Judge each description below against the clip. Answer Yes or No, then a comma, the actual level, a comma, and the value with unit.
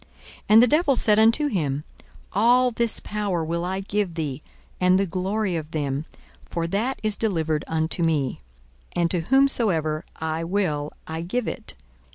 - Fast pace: No, average, 165 wpm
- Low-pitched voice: No, medium, 180 Hz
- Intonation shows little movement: No, average, 5.2 semitones